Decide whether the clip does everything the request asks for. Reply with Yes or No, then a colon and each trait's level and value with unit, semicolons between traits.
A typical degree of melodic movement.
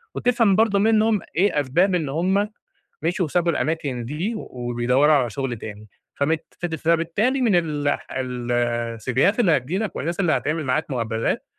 No: wide, 7.0 semitones